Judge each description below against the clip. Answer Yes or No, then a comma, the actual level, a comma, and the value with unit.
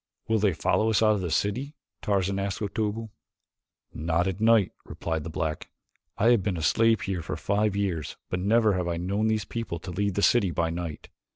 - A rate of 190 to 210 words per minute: Yes, fast, 205 wpm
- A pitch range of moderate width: Yes, average, 3.8 semitones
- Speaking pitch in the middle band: No, low, 100 Hz